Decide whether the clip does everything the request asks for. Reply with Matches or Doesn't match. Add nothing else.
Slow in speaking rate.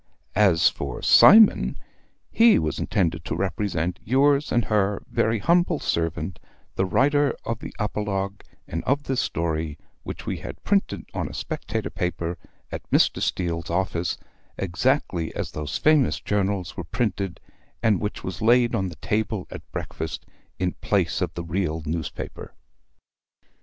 Doesn't match